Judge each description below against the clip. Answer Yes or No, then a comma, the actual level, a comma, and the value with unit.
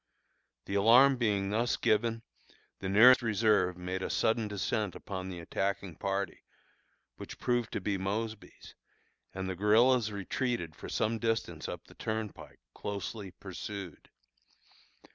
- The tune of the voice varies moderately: Yes, average, 3.0 semitones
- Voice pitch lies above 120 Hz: No, low, 105 Hz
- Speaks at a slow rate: Yes, slow, 130 wpm